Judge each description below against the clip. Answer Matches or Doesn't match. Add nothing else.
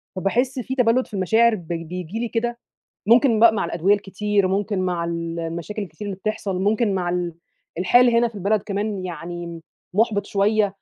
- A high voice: Matches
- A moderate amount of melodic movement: Matches